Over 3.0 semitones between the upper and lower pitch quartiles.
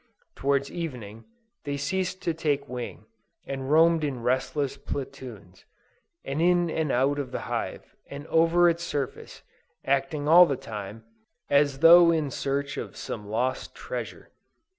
Yes: average, 3.8 semitones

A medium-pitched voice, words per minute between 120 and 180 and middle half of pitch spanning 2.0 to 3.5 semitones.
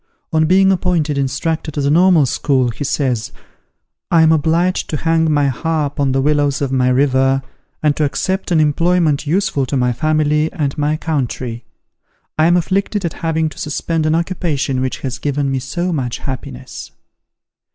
Yes: medium, 150 Hz; average, 170 wpm; average, 3.2 semitones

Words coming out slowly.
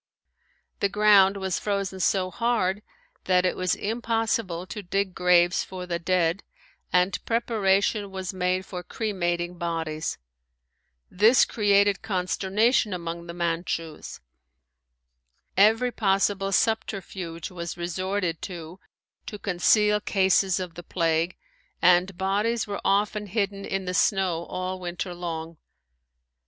Yes: slow, 120 wpm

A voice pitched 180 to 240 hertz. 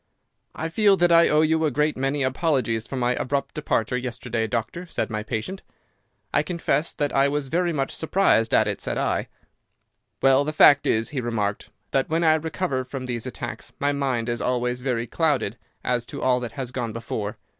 No: low, 130 Hz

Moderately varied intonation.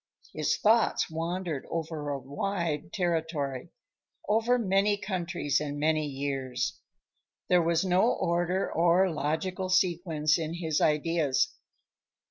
Yes: average, 3.7 semitones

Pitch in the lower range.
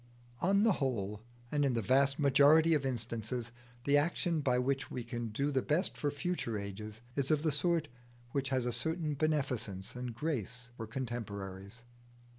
Yes: low, 130 Hz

